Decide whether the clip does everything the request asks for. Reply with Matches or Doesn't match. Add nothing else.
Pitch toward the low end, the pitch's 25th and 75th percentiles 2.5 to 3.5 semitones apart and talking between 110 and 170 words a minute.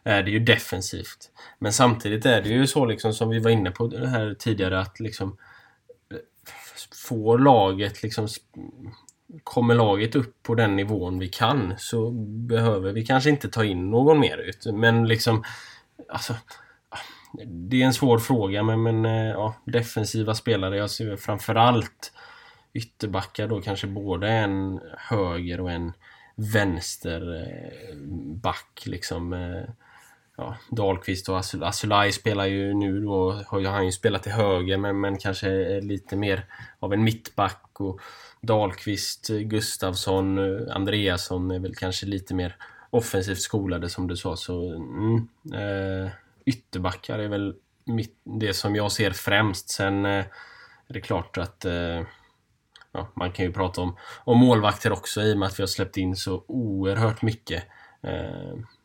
Matches